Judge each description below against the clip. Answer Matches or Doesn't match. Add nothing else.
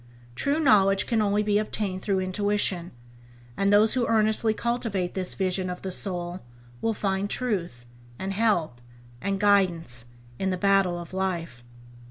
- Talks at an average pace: Matches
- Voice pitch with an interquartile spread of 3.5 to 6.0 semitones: Doesn't match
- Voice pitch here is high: Matches